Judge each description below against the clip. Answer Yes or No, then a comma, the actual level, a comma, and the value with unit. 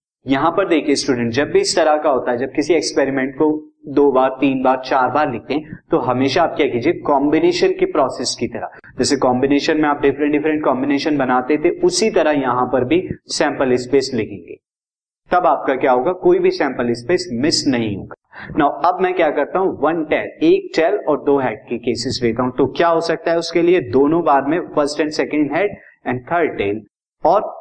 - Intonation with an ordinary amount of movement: Yes, average, 4.4 semitones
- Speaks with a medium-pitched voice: Yes, medium, 145 Hz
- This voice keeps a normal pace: No, fast, 210 wpm